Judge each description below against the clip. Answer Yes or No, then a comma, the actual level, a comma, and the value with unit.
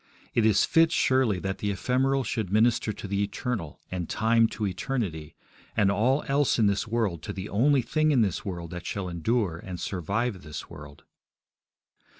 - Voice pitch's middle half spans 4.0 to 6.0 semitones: Yes, average, 5.0 semitones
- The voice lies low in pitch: Yes, low, 105 Hz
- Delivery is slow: No, average, 175 wpm